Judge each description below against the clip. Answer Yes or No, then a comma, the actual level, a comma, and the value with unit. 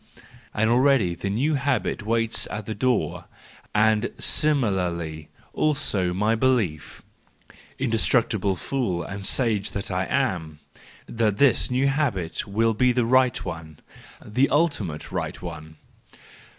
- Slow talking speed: Yes, slow, 120 wpm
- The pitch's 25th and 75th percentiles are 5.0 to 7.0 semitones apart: Yes, wide, 5.6 semitones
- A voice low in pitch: Yes, low, 110 Hz